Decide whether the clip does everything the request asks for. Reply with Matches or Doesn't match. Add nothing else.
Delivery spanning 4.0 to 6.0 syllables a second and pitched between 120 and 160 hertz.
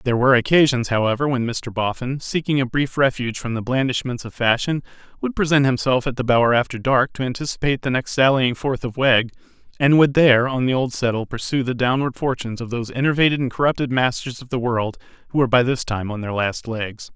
Doesn't match